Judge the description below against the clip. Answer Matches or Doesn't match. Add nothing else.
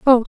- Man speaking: Doesn't match